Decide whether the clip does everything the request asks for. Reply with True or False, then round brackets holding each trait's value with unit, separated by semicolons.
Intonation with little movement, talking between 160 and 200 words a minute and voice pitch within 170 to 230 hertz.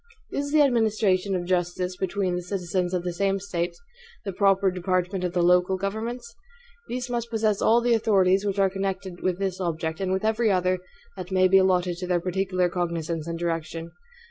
True (2.0 semitones; 190 wpm; 185 Hz)